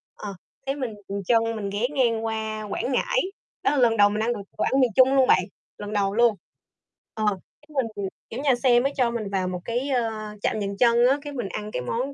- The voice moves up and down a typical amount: Yes, average, 3.8 semitones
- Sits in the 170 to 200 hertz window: No, high, 230 Hz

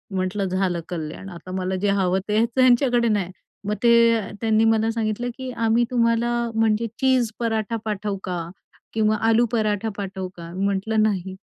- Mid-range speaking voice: No, high, 215 Hz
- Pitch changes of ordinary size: Yes, average, 3.3 semitones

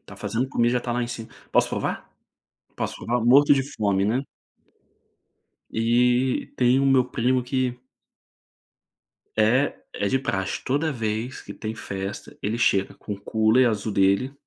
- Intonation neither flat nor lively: Yes, average, 3.0 semitones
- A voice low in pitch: Yes, low, 120 Hz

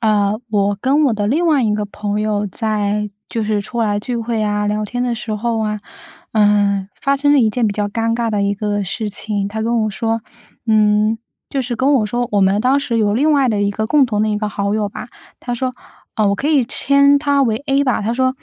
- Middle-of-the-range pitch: No, high, 220 Hz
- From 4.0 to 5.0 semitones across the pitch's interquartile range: No, average, 3.0 semitones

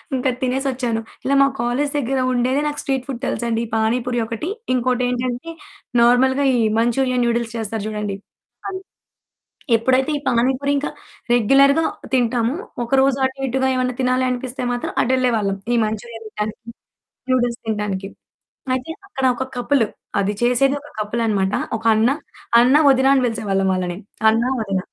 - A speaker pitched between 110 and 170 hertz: No, high, 245 Hz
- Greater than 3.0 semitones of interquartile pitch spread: No, average, 2.7 semitones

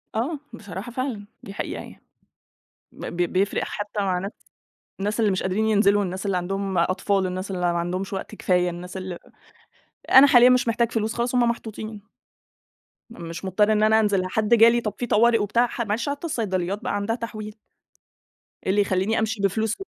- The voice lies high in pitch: Yes, high, 205 Hz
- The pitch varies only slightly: No, average, 3.2 semitones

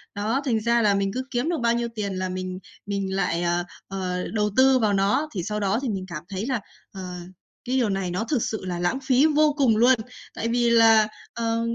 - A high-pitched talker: Yes, high, 215 Hz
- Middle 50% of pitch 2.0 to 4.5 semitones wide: Yes, average, 4.0 semitones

